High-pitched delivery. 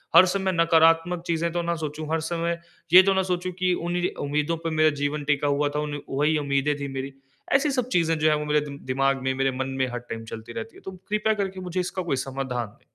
No: medium, 155 Hz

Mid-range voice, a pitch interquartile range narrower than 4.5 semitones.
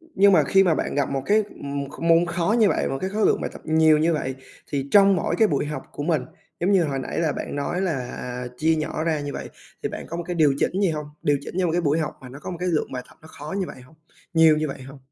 Yes: medium, 160 Hz; average, 3.7 semitones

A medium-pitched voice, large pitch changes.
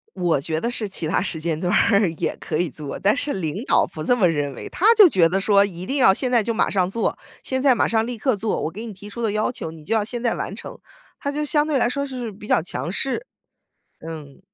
No: high, 205 Hz; wide, 6.4 semitones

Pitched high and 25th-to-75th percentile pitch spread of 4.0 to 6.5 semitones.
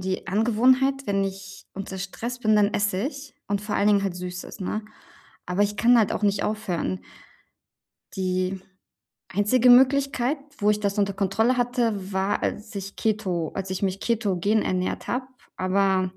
No: high, 205 Hz; average, 2.9 semitones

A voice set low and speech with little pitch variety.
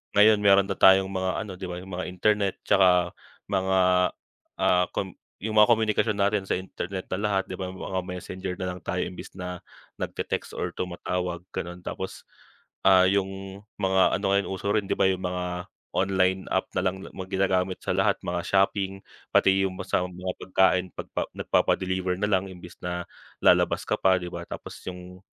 Yes: very low, 95 Hz; narrow, 1.2 semitones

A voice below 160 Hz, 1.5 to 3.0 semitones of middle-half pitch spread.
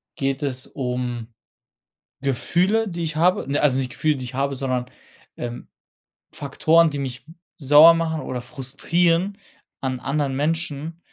No: medium, 140 Hz; average, 4.1 semitones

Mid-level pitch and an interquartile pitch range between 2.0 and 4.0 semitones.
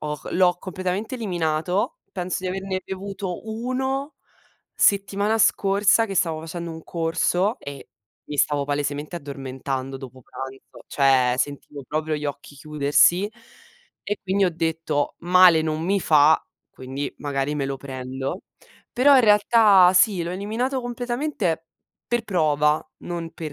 No: medium, 170 Hz; wide, 5.5 semitones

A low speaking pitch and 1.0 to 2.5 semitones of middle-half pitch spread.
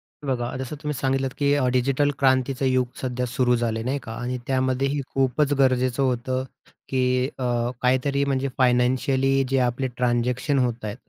Yes: low, 130 Hz; narrow, 1.6 semitones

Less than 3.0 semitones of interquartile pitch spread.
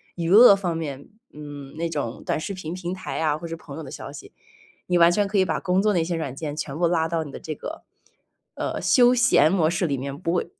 No: average, 3.5 semitones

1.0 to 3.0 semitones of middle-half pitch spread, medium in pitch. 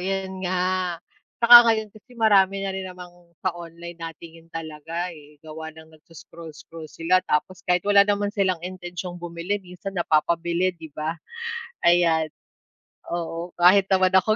Yes: narrow, 2.4 semitones; medium, 175 Hz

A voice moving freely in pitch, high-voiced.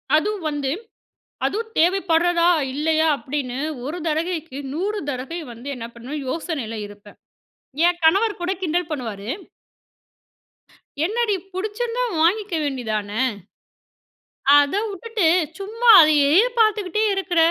Yes: wide, 5.9 semitones; very high, 325 Hz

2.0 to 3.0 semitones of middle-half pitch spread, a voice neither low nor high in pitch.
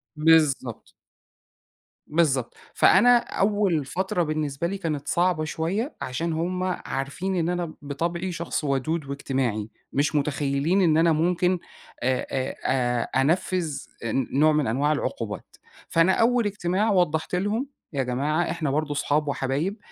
No: average, 4.4 semitones; medium, 155 Hz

